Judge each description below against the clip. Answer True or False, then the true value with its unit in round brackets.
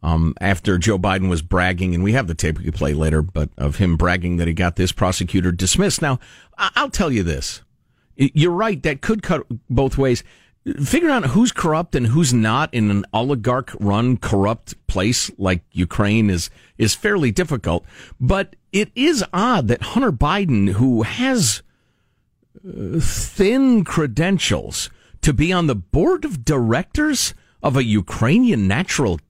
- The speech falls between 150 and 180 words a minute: True (160 wpm)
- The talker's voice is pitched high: False (115 Hz)